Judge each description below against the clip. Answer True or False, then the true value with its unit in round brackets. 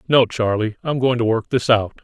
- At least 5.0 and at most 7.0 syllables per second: True (5.3 syllables/s)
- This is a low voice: True (120 Hz)